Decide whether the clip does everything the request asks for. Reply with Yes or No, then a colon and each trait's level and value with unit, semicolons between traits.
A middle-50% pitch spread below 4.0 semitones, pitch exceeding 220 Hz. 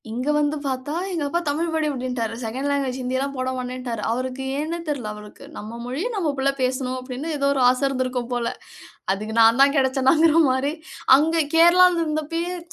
Yes: average, 3.4 semitones; very high, 265 Hz